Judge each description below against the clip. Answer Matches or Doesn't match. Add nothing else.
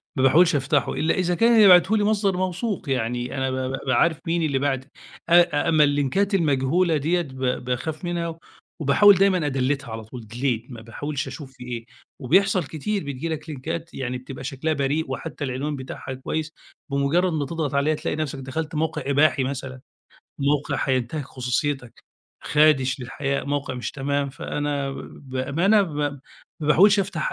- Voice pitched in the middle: Matches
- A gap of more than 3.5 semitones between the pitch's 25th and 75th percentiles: Matches